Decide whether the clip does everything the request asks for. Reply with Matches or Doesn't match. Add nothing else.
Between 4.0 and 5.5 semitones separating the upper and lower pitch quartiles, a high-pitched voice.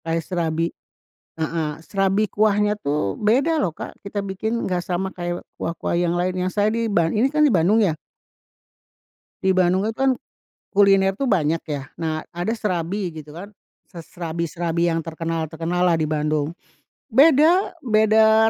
Doesn't match